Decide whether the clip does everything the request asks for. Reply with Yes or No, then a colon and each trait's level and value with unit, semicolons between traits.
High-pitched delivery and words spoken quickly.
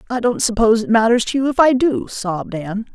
Yes: high, 225 Hz; fast, 245 wpm